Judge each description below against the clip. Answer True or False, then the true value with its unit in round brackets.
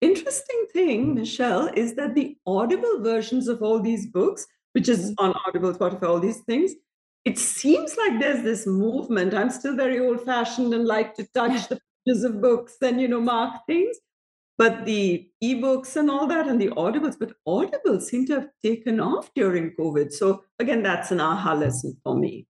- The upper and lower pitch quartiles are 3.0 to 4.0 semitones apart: False (4.6 semitones)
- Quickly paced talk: False (190 wpm)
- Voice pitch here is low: False (240 Hz)